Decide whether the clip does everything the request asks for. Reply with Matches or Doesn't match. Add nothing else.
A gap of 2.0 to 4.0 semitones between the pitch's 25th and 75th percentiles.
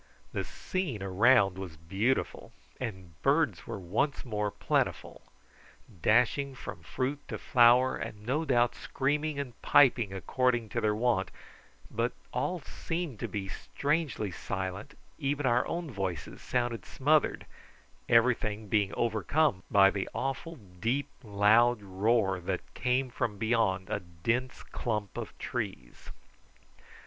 Doesn't match